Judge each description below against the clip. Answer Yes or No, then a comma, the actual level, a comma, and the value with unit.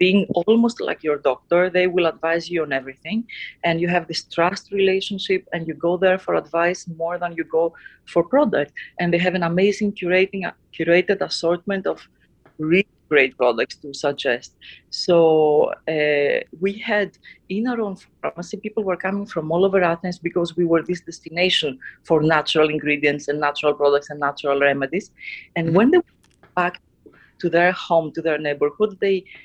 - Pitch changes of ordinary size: Yes, average, 3.1 semitones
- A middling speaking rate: Yes, average, 170 wpm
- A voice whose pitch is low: No, medium, 175 Hz